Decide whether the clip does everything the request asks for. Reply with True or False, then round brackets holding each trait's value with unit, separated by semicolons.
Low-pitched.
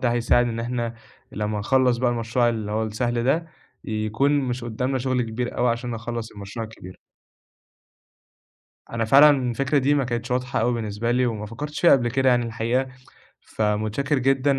True (120 Hz)